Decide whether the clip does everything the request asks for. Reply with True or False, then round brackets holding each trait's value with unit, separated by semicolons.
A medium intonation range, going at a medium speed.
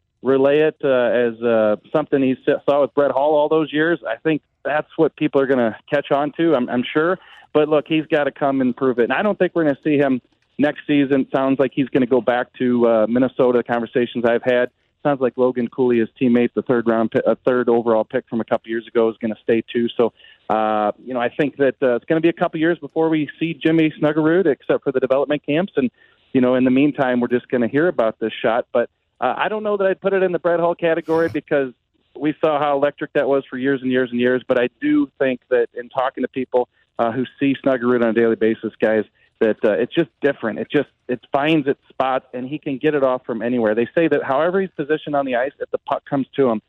False (4.0 semitones; 260 wpm)